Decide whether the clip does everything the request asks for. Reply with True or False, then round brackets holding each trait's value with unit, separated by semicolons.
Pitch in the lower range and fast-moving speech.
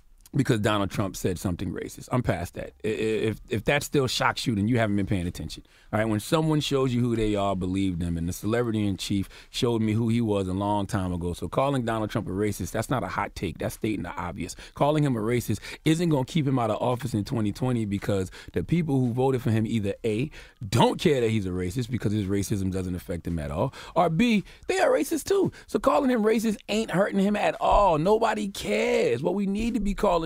True (115 Hz; 240 wpm)